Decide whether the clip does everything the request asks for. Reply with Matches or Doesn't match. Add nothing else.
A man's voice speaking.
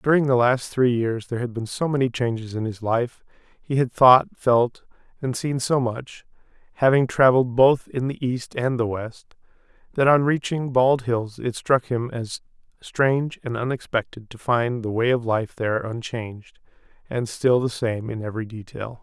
Matches